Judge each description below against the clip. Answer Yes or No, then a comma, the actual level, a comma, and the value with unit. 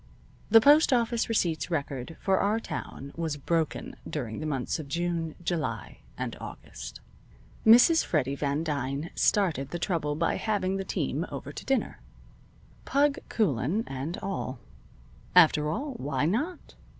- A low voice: No, medium, 165 Hz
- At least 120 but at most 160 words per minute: Yes, average, 140 wpm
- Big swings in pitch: Yes, wide, 6.5 semitones